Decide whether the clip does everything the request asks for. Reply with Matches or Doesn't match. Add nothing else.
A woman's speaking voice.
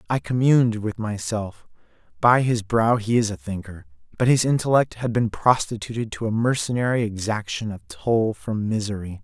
Doesn't match